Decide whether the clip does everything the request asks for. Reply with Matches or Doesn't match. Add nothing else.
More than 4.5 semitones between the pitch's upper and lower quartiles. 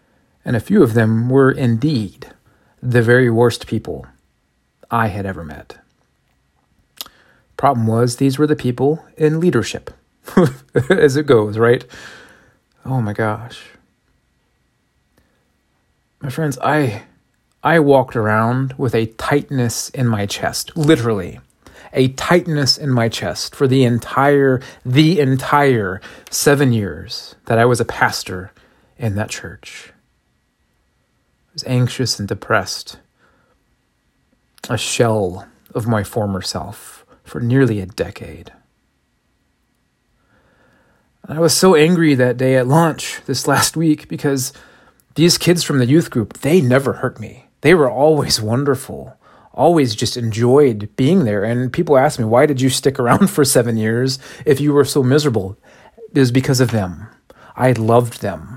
Doesn't match